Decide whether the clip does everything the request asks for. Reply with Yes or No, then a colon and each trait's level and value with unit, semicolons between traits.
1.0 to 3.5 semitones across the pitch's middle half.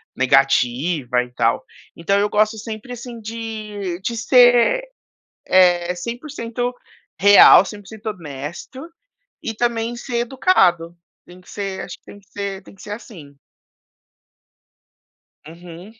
No: average, 4.9 semitones